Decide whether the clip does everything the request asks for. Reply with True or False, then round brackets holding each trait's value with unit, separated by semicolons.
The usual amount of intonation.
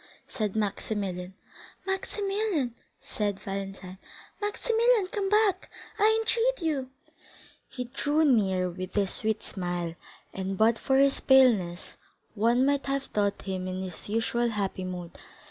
False (7.8 semitones)